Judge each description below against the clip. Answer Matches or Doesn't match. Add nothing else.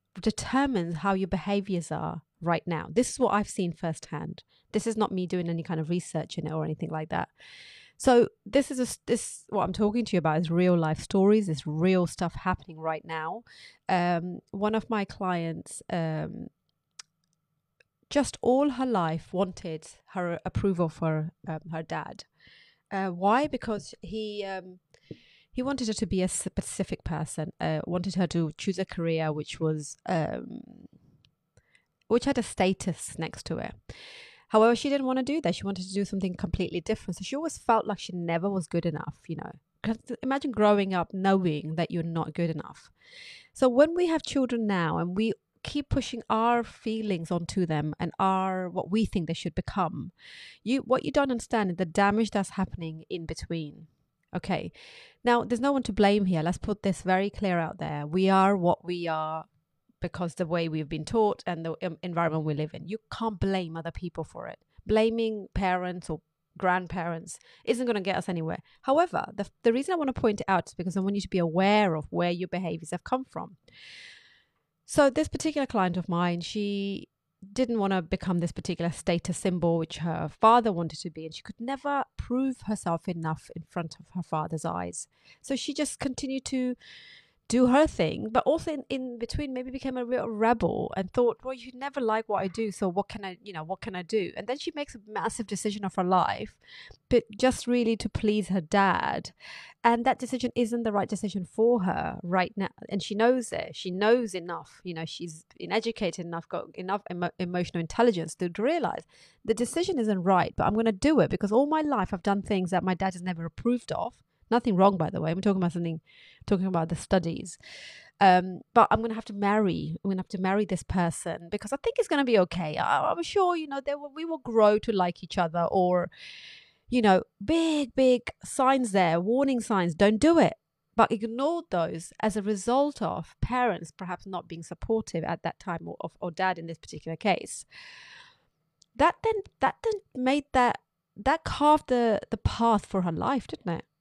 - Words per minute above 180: Matches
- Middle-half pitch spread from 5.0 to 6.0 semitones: Matches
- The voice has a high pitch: Matches